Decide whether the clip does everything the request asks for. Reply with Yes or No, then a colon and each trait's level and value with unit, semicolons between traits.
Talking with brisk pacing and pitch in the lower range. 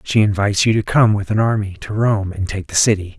Yes: fast, 265 wpm; low, 105 Hz